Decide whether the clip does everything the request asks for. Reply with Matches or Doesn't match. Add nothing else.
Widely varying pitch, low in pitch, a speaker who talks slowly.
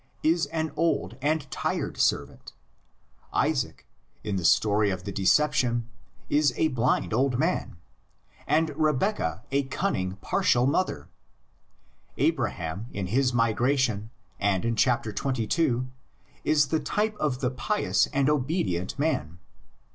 Matches